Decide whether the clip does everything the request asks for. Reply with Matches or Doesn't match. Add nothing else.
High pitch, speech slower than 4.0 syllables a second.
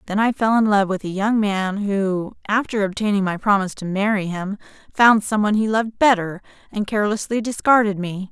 Doesn't match